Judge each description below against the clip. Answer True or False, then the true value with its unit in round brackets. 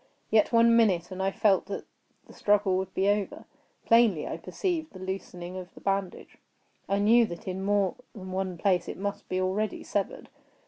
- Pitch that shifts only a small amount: True (2.0 semitones)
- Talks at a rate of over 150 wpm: True (185 wpm)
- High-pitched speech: True (195 Hz)